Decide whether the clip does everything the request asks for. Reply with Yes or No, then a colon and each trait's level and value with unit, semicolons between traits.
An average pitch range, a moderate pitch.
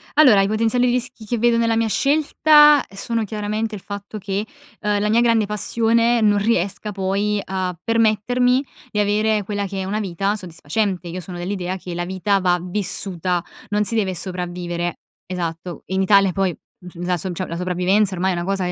No: average, 3.2 semitones; high, 200 Hz